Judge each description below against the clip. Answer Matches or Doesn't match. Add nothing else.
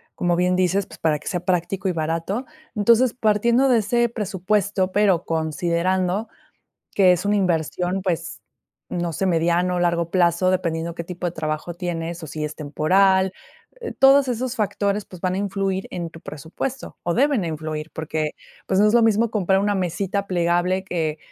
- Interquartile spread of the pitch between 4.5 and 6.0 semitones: Doesn't match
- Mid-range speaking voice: Matches